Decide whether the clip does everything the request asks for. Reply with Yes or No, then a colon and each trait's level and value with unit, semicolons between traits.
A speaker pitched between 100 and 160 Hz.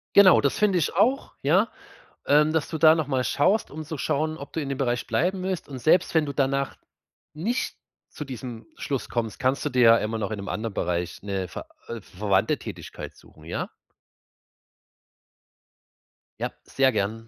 Yes: low, 135 Hz